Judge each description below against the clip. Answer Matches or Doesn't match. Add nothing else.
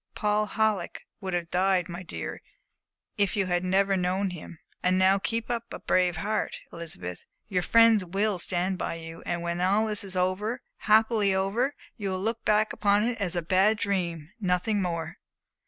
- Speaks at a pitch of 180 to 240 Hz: Matches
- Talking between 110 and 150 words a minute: Doesn't match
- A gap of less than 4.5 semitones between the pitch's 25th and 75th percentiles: Matches